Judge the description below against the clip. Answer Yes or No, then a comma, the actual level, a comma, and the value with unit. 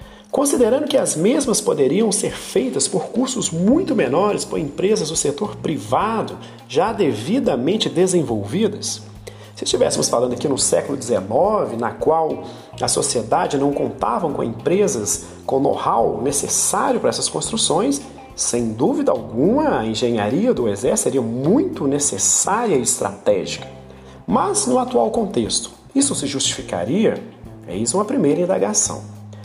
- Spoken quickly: No, average, 130 wpm